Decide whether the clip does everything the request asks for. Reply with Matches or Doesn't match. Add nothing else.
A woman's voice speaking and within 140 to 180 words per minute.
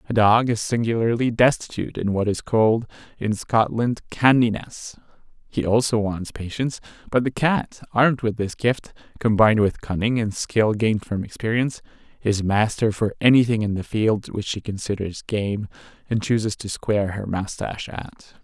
Doesn't match